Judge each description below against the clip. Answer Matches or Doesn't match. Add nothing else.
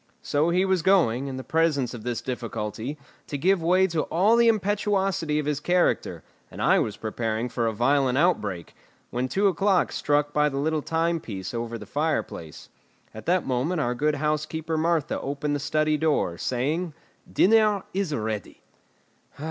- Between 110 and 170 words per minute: Matches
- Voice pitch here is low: Doesn't match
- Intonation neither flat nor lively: Doesn't match